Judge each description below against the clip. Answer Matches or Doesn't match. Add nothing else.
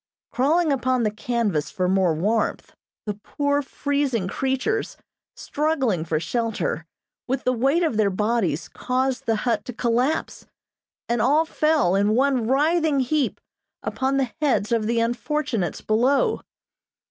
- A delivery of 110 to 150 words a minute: Matches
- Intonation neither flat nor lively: Matches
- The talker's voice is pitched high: Matches